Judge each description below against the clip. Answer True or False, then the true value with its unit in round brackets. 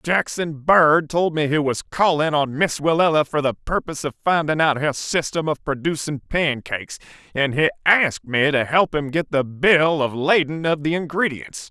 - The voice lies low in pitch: False (155 Hz)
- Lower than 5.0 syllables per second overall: True (4.8 syllables/s)